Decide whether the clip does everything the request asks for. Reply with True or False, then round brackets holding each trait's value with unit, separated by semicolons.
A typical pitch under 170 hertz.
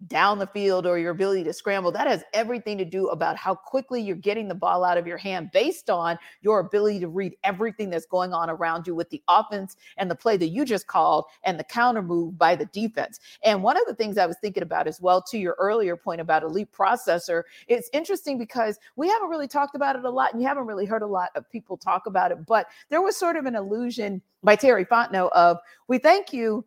False (205 Hz)